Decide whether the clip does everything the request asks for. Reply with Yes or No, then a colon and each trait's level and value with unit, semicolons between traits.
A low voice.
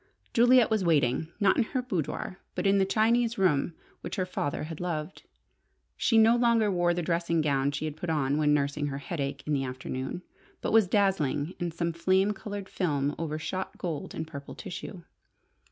No: medium, 170 Hz